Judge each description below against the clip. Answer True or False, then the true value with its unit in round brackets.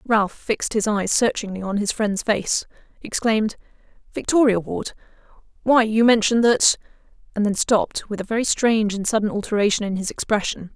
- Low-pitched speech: False (215 Hz)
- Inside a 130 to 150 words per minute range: False (160 wpm)